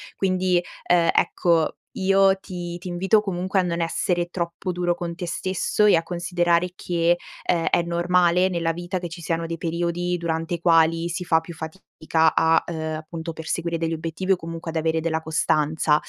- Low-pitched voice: No, medium, 170 Hz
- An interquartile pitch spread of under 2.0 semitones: Yes, narrow, 1.4 semitones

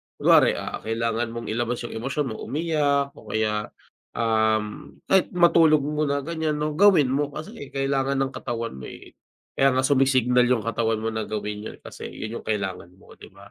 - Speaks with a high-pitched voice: No, low, 125 Hz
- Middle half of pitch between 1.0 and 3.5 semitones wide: No, average, 4.3 semitones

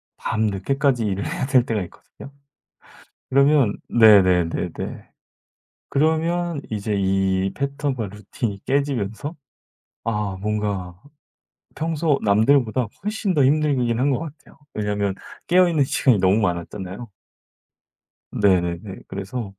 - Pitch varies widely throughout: Yes, wide, 6.2 semitones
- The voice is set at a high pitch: No, low, 110 Hz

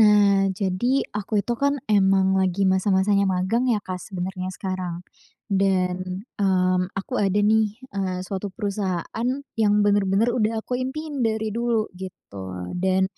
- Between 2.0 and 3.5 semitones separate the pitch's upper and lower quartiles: Yes, narrow, 2.5 semitones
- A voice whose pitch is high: Yes, high, 195 Hz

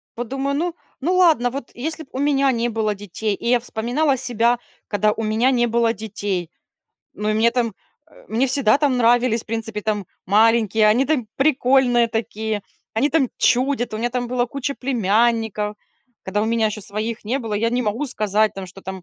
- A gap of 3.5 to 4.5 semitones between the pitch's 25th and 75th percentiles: No, average, 3.1 semitones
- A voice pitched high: Yes, high, 235 Hz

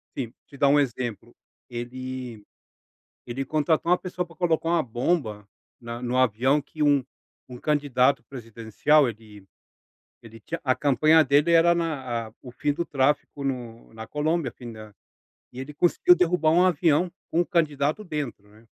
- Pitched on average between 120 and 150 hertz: Yes, medium, 140 Hz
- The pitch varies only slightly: No, average, 4.8 semitones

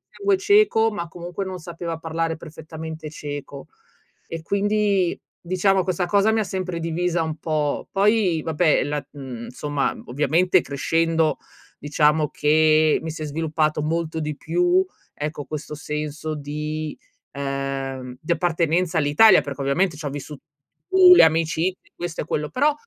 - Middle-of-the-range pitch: Yes, medium, 160 Hz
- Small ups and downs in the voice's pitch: No, average, 3.0 semitones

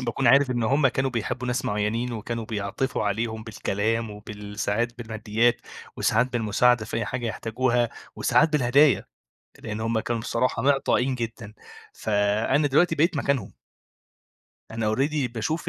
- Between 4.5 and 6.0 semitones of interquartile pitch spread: No, average, 2.9 semitones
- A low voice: Yes, low, 115 Hz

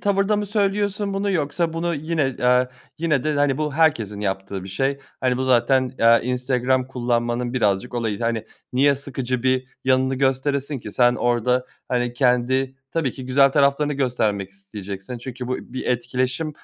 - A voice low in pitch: Yes, low, 130 Hz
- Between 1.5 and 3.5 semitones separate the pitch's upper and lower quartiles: Yes, average, 2.9 semitones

